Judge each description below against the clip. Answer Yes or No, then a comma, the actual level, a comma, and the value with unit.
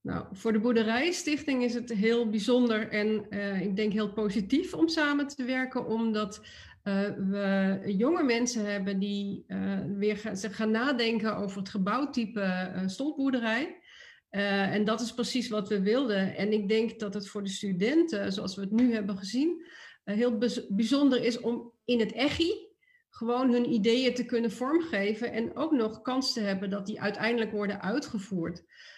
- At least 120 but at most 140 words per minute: No, average, 175 wpm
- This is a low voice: No, high, 225 Hz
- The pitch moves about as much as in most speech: Yes, average, 3.5 semitones